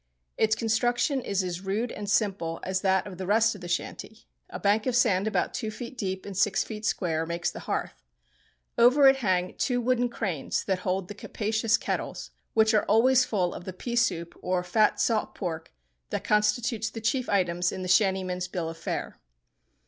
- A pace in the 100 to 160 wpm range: No, average, 195 wpm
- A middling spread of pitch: Yes, average, 3.8 semitones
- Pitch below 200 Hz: No, high, 205 Hz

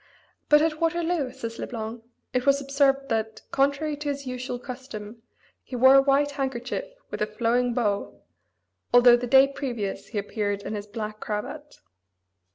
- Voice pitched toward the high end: Yes, very high, 250 Hz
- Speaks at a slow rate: No, average, 165 wpm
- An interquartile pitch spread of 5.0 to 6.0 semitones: No, average, 3.8 semitones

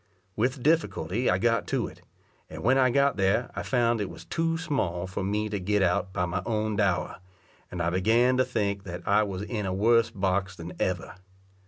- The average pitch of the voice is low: Yes, low, 105 Hz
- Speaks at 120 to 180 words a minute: No, fast, 205 wpm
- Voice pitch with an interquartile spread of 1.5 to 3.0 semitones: No, average, 4.2 semitones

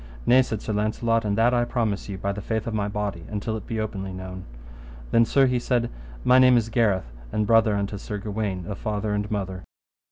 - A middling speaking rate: No, fast, 220 wpm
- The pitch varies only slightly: Yes, narrow, 2.3 semitones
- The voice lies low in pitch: Yes, low, 105 Hz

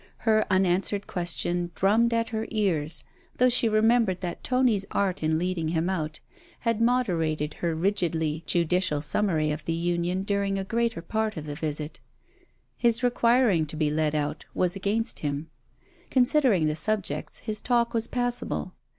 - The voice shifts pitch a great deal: Yes, wide, 5.9 semitones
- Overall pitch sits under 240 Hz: Yes, medium, 185 Hz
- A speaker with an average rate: Yes, average, 160 wpm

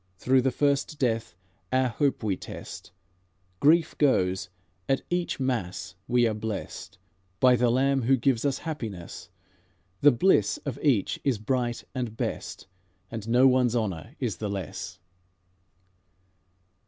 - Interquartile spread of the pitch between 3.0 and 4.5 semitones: Yes, average, 3.8 semitones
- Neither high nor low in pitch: No, low, 125 Hz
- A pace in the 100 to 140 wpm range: Yes, slow, 135 wpm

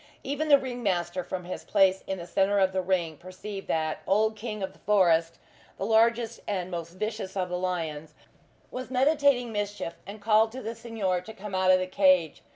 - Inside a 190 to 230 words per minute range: Yes, average, 200 wpm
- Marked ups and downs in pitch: No, average, 3.5 semitones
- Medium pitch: No, high, 195 Hz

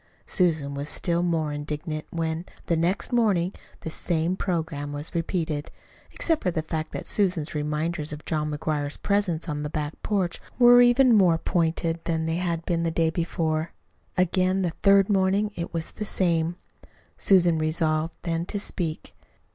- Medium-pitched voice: Yes, medium, 165 Hz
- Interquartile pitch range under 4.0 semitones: Yes, average, 2.8 semitones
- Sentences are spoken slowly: No, average, 165 wpm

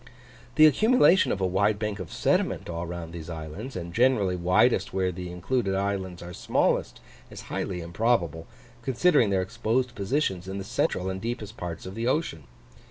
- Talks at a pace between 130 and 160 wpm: No, average, 170 wpm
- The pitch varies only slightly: No, average, 5.1 semitones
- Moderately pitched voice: No, very low, 95 Hz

